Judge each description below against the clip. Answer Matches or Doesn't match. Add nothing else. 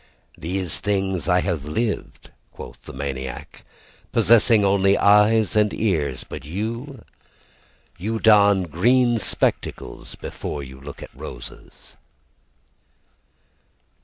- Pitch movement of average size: Doesn't match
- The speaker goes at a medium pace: Doesn't match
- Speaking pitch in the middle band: Doesn't match